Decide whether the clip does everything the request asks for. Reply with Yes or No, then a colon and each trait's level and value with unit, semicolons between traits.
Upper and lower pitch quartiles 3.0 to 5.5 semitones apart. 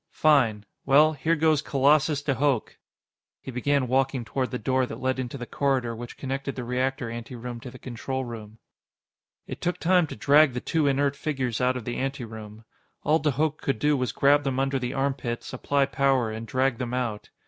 No: narrow, 2.5 semitones